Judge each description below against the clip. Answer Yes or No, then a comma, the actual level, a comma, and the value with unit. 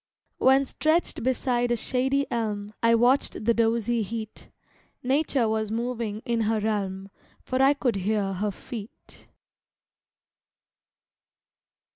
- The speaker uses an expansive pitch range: No, average, 3.0 semitones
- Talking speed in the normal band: No, slow, 115 wpm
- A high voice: Yes, high, 230 Hz